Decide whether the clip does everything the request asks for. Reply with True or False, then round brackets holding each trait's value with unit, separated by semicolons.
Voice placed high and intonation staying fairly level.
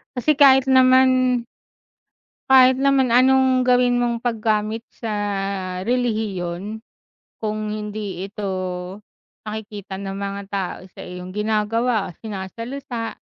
False (220 Hz; 4.0 semitones)